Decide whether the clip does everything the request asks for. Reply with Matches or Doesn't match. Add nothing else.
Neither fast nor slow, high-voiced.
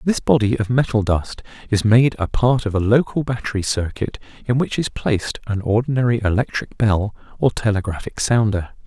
Doesn't match